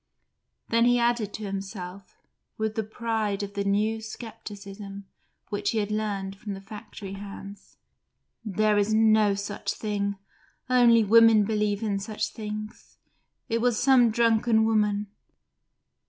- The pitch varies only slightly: Yes, narrow, 1.8 semitones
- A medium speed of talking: No, slow, 130 wpm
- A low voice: No, high, 215 Hz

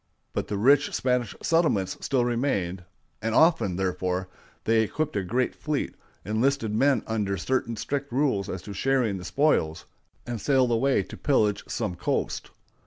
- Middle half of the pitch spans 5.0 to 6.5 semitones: Yes, wide, 5.6 semitones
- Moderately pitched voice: No, low, 115 Hz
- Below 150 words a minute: No, average, 155 wpm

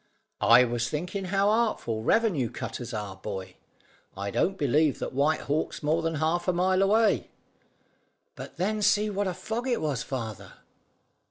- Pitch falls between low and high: Yes, medium, 160 Hz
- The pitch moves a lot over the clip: Yes, wide, 8.1 semitones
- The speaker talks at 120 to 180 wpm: Yes, average, 160 wpm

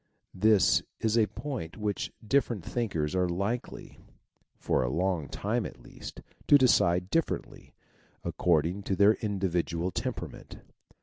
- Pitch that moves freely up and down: No, average, 4.2 semitones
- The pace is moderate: No, slow, 130 wpm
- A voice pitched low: Yes, very low, 95 Hz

